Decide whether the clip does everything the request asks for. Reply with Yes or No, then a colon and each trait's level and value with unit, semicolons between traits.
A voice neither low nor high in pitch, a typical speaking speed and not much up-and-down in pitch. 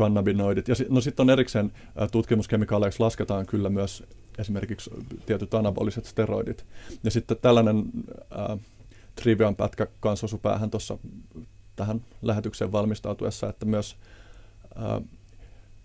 No: low, 105 Hz; average, 105 wpm; narrow, 1.8 semitones